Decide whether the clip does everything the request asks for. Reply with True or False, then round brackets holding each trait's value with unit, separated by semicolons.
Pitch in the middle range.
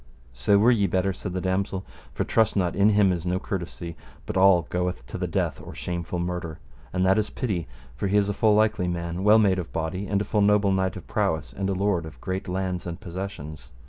False (95 Hz)